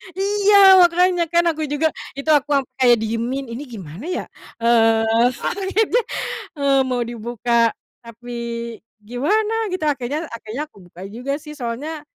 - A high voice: Yes, very high, 275 Hz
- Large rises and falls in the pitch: Yes, wide, 6.1 semitones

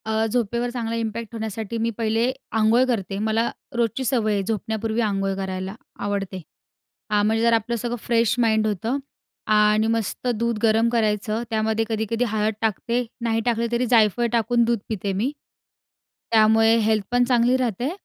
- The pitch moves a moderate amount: No, narrow, 1.6 semitones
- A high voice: Yes, high, 225 Hz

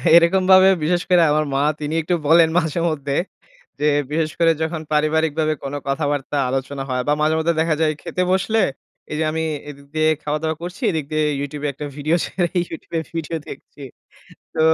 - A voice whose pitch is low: No, medium, 155 Hz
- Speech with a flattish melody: Yes, narrow, 2.3 semitones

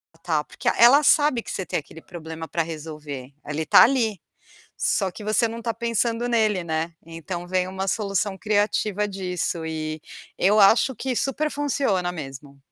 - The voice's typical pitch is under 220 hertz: Yes, high, 190 Hz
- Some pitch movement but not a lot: No, wide, 5.8 semitones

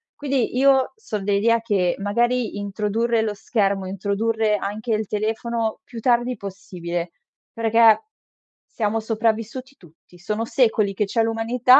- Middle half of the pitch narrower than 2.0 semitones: No, narrow, 2.6 semitones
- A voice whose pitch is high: Yes, high, 220 Hz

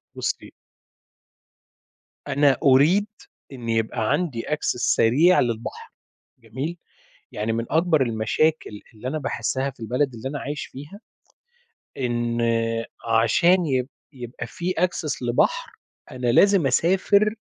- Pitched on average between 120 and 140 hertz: Yes, low, 135 Hz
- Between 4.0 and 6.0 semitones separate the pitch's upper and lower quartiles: Yes, wide, 5.4 semitones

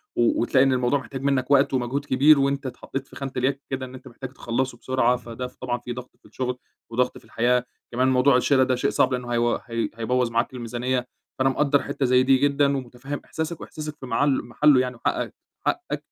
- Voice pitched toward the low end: Yes, low, 130 Hz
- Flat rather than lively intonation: Yes, narrow, 1.9 semitones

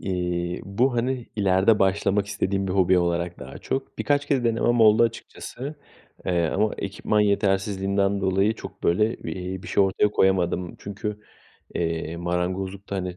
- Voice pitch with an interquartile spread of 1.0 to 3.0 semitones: Yes, average, 2.7 semitones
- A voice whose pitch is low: Yes, very low, 95 Hz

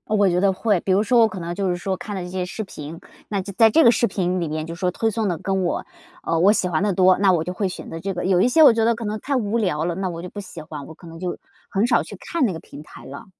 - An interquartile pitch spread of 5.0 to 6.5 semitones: No, average, 3.4 semitones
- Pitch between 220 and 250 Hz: No, high, 190 Hz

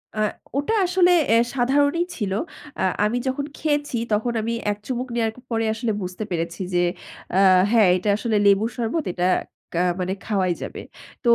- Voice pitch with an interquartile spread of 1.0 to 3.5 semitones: No, average, 4.9 semitones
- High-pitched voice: Yes, high, 225 Hz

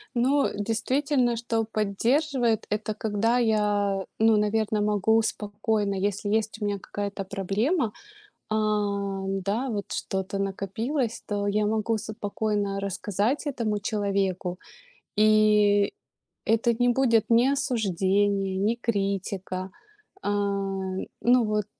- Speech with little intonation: Yes, narrow, 2.3 semitones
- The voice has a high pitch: Yes, high, 210 Hz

